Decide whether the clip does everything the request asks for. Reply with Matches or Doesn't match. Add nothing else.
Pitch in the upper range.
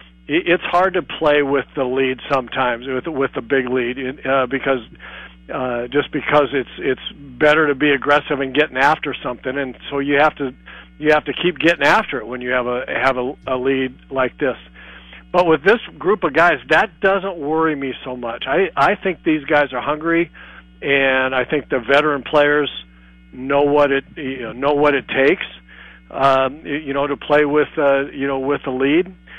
Doesn't match